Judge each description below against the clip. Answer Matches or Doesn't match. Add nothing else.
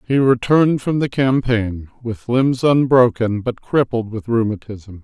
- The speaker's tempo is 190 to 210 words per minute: Doesn't match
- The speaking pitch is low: Matches